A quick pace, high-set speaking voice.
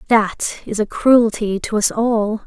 No: average, 170 wpm; high, 220 Hz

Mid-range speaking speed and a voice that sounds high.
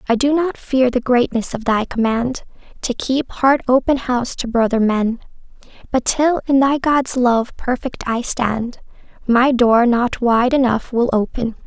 Yes: average, 170 wpm; high, 245 Hz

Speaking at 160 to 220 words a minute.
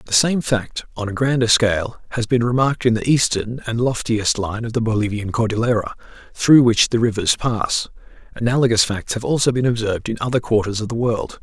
Yes: average, 195 wpm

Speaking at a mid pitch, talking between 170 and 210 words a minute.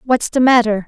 No: high, 235 Hz; fast, 205 wpm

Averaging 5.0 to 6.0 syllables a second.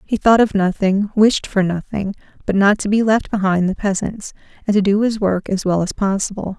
Yes: 5.2 syllables/s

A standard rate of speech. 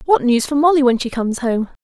No: fast, 260 wpm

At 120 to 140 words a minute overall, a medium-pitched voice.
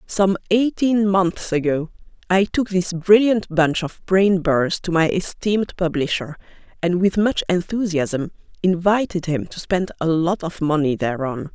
No: average, 150 wpm; medium, 180 Hz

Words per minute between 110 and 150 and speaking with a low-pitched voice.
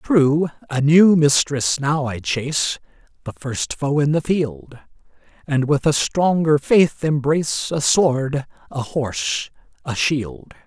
No: average, 140 wpm; medium, 145 Hz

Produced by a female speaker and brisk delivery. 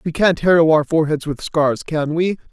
No: male; fast, 215 wpm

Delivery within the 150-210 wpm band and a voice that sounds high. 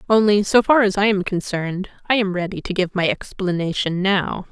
Yes: average, 200 wpm; high, 195 Hz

